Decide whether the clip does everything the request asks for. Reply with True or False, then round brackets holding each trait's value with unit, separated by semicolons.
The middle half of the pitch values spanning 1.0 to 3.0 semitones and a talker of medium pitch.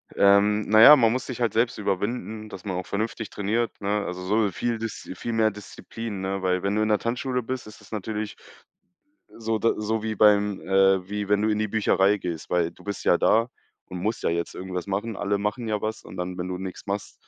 False (2.5 semitones; 105 Hz)